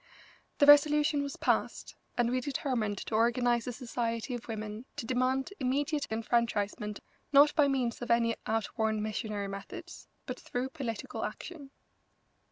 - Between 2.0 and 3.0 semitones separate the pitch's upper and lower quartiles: No, average, 3.9 semitones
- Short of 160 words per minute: Yes, average, 140 wpm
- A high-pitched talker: Yes, high, 245 Hz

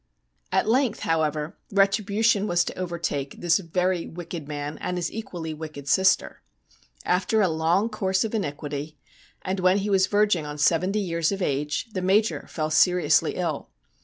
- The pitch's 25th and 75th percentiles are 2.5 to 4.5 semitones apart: Yes, average, 3.9 semitones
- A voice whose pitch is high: No, medium, 180 Hz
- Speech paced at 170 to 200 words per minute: No, average, 160 wpm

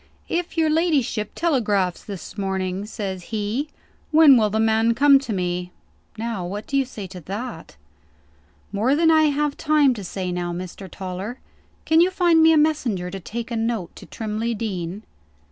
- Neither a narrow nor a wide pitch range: No, wide, 7.0 semitones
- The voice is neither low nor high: No, high, 220 Hz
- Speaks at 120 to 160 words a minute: No, average, 175 wpm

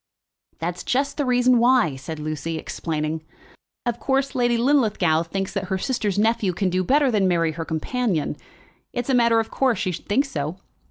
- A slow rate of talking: No, average, 180 wpm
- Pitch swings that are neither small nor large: No, wide, 7.0 semitones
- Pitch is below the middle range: No, high, 205 Hz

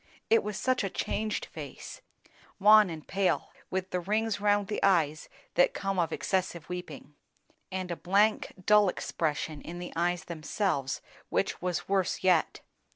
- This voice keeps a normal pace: Yes, average, 155 wpm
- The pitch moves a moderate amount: Yes, average, 3.3 semitones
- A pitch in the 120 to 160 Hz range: No, medium, 185 Hz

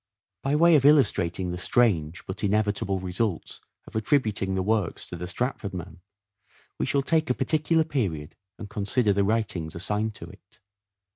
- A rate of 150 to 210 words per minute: Yes, average, 160 wpm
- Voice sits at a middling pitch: No, low, 105 Hz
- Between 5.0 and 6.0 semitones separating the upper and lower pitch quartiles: Yes, wide, 5.4 semitones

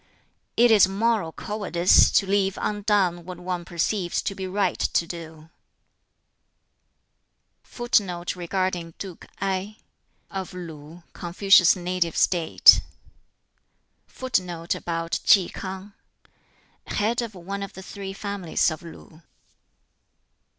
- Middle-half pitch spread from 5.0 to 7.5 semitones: No, average, 2.7 semitones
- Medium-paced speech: No, slow, 95 wpm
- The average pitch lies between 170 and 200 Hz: Yes, medium, 185 Hz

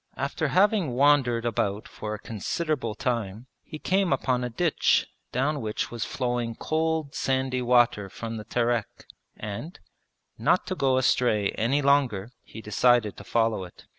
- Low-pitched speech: Yes, low, 125 Hz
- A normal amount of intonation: Yes, average, 4.0 semitones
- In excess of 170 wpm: No, average, 150 wpm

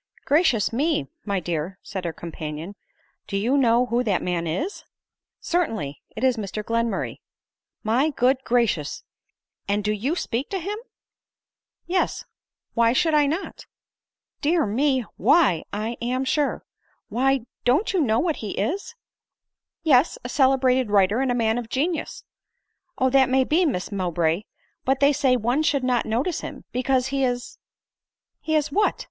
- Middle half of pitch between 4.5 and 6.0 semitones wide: Yes, average, 5.3 semitones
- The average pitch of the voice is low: No, very high, 250 Hz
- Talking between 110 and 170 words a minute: No, average, 185 wpm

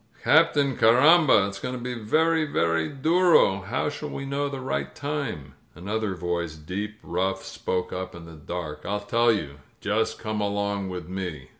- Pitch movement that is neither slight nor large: No, wide, 7.4 semitones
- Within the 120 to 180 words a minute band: Yes, average, 170 wpm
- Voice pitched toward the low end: Yes, low, 105 Hz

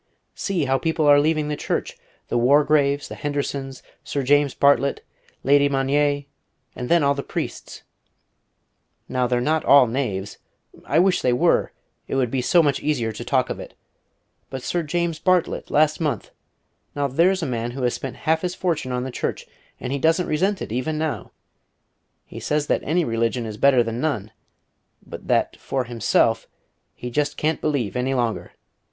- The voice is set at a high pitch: No, medium, 140 Hz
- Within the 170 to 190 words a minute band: Yes, average, 175 wpm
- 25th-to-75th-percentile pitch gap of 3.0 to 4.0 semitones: Yes, average, 3.6 semitones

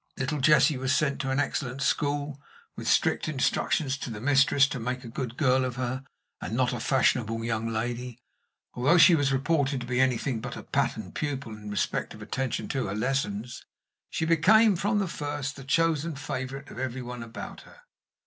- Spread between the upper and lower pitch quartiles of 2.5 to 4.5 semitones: Yes, average, 2.8 semitones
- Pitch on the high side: No, low, 130 Hz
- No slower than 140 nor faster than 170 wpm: No, average, 190 wpm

